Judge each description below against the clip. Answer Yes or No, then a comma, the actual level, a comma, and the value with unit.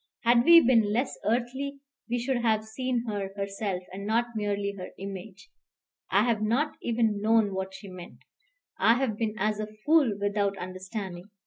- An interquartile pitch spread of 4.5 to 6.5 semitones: No, average, 3.2 semitones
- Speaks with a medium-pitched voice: No, high, 215 Hz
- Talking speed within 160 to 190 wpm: Yes, average, 165 wpm